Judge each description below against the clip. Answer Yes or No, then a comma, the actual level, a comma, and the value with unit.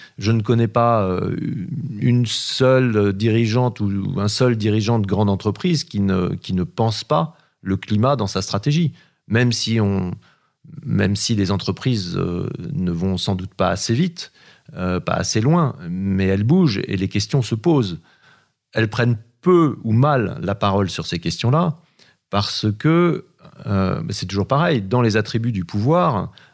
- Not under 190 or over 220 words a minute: No, average, 160 wpm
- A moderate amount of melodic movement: No, wide, 5.7 semitones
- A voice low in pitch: Yes, low, 115 Hz